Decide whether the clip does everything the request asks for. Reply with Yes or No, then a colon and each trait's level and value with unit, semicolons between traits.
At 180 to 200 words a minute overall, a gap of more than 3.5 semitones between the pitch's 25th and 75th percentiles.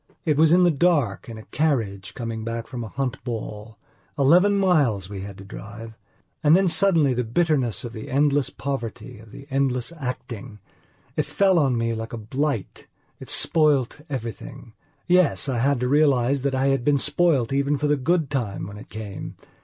Yes: average, 185 wpm; average, 4.7 semitones